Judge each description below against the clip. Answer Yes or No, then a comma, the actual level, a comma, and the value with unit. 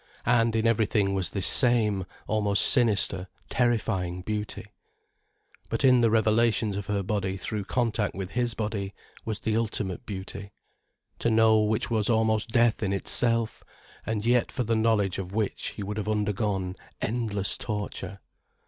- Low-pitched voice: Yes, low, 105 Hz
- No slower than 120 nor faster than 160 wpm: Yes, average, 150 wpm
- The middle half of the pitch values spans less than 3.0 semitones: Yes, narrow, 2.4 semitones